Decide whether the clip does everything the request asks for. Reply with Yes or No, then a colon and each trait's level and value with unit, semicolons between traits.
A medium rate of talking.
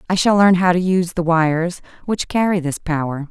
No: fast, 220 wpm